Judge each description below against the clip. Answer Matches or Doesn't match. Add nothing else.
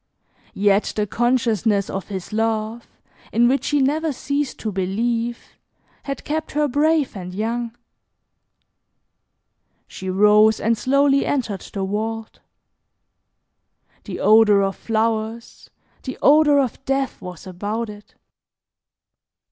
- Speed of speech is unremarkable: Doesn't match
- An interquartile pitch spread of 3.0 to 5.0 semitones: Matches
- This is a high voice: Matches